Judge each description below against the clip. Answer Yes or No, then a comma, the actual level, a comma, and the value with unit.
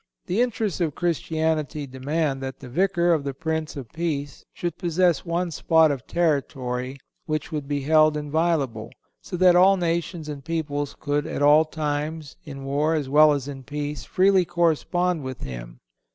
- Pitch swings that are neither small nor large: Yes, average, 3.2 semitones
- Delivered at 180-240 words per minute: No, average, 165 wpm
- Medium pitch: Yes, medium, 155 Hz